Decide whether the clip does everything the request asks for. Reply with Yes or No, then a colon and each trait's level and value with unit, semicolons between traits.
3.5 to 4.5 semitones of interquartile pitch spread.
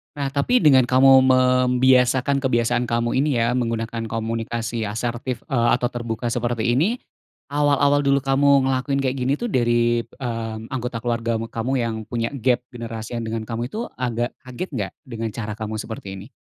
No: narrow, 2.4 semitones